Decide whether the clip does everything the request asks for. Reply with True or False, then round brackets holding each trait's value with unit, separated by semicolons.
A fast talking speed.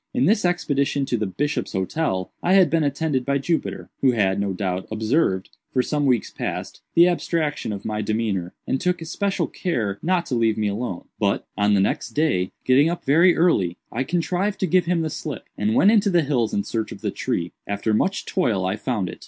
True (210 wpm)